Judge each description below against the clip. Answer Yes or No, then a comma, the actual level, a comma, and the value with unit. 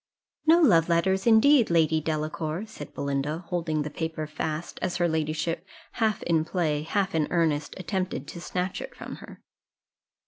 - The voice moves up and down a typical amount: Yes, average, 3.2 semitones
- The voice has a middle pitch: Yes, medium, 165 Hz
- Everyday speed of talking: Yes, average, 160 wpm